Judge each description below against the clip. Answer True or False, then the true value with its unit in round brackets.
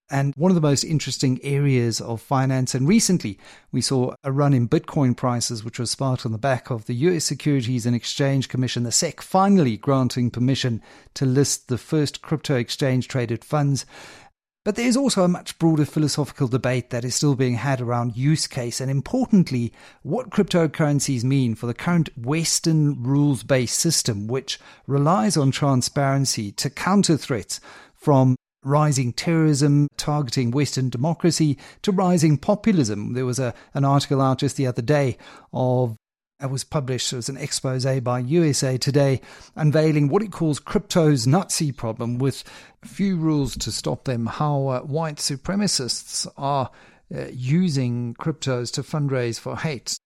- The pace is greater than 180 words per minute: False (160 wpm)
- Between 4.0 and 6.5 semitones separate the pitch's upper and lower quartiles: False (3.5 semitones)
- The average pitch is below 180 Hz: True (140 Hz)